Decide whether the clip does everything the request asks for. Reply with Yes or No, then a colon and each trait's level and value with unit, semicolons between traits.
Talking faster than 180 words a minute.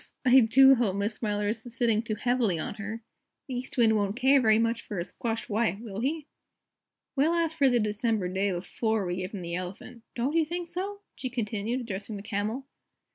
Yes: fast, 205 wpm